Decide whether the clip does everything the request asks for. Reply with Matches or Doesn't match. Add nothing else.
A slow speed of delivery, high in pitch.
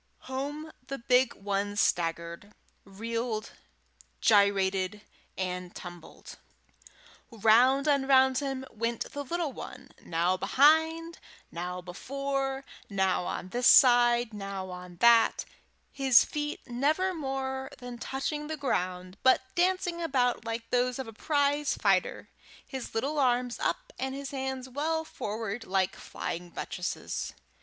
Matches